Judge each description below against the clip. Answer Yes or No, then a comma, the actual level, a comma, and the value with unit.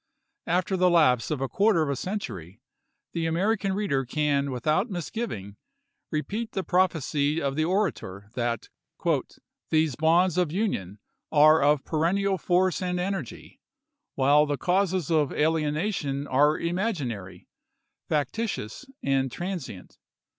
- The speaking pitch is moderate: Yes, medium, 155 Hz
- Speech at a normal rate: No, slow, 125 wpm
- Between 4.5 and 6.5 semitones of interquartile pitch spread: Yes, average, 5.2 semitones